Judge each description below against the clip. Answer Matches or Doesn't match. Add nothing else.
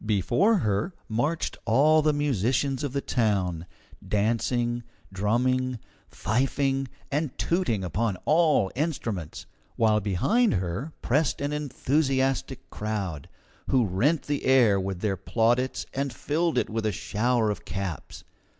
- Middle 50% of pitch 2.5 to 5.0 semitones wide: Doesn't match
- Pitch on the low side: Matches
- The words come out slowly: Matches